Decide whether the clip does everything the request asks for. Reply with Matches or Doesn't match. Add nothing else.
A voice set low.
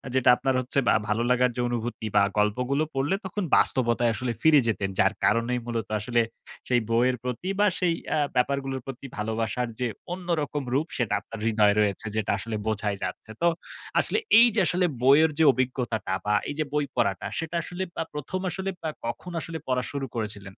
Matches